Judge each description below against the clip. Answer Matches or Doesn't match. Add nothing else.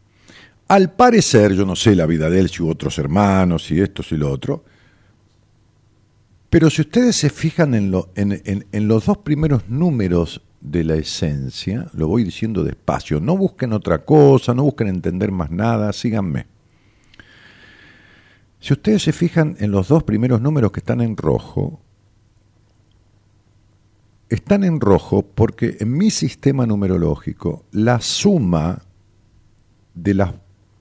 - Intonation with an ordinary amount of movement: Matches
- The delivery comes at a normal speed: Matches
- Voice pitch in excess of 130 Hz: Doesn't match